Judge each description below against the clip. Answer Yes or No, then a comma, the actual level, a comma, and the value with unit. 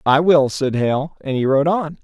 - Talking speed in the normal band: No, fast, 235 wpm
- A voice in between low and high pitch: Yes, medium, 145 Hz